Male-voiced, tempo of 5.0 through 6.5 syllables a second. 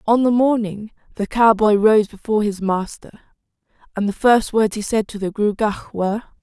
No: female; 5.2 syllables/s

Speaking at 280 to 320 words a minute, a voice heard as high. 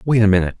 No: fast, 300 wpm; low, 105 Hz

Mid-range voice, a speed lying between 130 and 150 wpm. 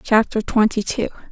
No: high, 220 Hz; slow, 135 wpm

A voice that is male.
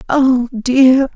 No: female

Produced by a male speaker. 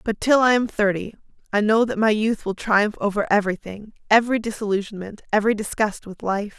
No: female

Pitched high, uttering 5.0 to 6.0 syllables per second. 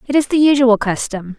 Yes: high, 245 Hz; 5.6 syllables/s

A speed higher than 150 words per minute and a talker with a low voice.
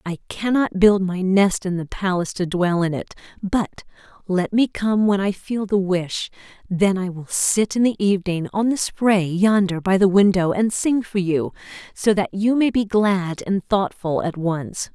No: average, 195 wpm; high, 195 Hz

